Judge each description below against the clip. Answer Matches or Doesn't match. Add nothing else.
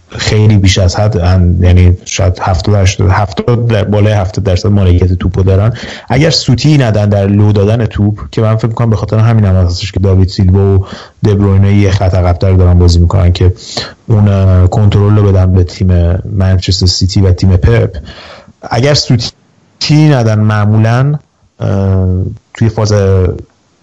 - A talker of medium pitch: Doesn't match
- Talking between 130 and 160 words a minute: Matches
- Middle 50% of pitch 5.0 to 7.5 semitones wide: Doesn't match